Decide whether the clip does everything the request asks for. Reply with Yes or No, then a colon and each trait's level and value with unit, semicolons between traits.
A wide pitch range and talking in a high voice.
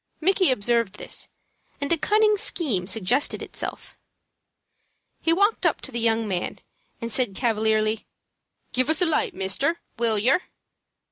Yes: wide, 7.0 semitones; high, 240 Hz